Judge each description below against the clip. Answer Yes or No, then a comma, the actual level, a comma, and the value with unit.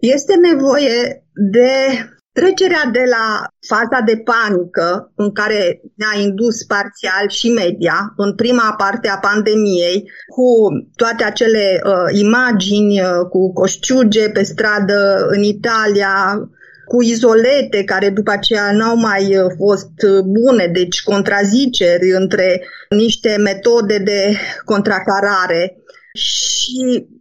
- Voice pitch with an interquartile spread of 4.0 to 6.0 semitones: No, average, 3.3 semitones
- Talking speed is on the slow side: Yes, slow, 110 wpm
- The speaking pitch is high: Yes, high, 210 Hz